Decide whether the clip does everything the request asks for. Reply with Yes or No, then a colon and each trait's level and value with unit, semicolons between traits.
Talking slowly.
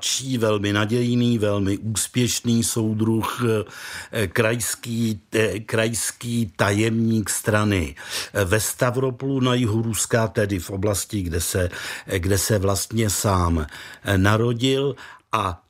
Yes: slow, 100 wpm